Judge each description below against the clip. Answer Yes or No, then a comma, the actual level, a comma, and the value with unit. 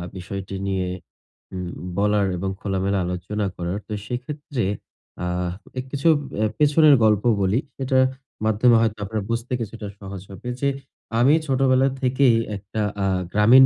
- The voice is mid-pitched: No, low, 110 Hz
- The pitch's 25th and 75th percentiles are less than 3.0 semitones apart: No, average, 4.9 semitones